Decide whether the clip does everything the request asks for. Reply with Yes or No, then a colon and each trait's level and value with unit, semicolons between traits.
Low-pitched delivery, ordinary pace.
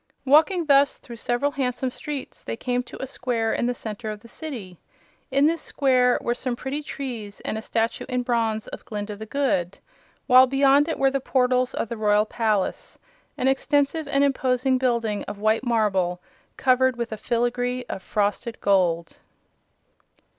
No: high, 245 Hz; average, 170 wpm